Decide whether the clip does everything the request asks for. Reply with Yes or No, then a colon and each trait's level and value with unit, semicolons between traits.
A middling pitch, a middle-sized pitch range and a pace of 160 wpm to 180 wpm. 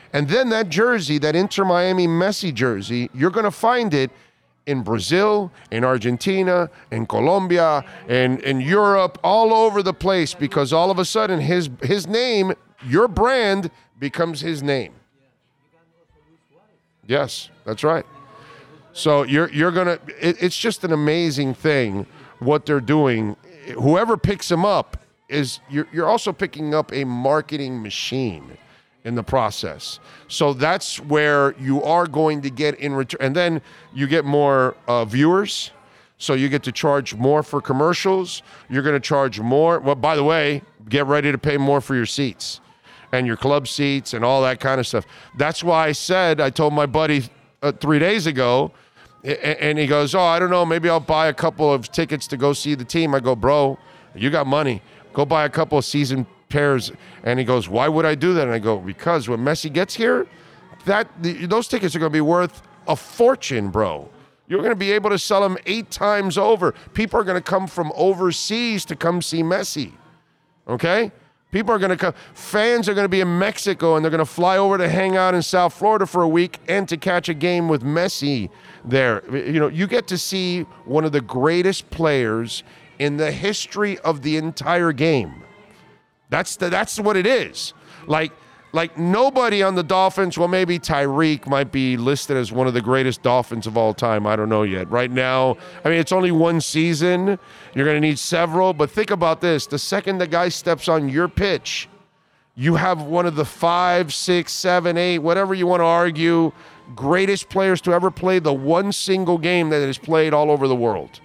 No: medium, 160 Hz; average, 4.5 semitones; average, 195 wpm